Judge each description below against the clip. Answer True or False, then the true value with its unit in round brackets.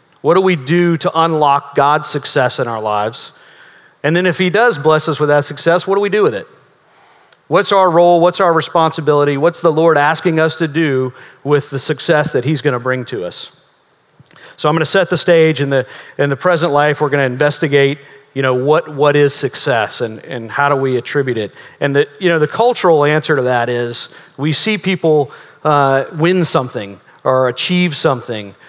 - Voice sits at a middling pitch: True (150 Hz)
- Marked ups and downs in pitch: False (3.5 semitones)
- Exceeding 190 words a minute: True (205 wpm)